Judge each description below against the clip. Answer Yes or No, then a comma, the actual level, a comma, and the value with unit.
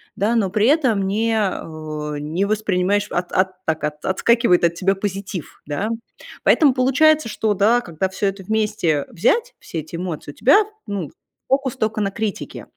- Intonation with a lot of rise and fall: No, average, 3.9 semitones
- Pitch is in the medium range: No, high, 200 Hz